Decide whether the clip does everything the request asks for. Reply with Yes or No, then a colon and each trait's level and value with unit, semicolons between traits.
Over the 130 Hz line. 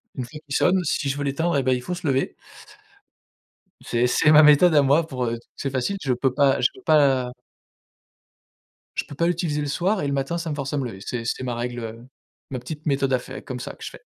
Yes: medium, 140 Hz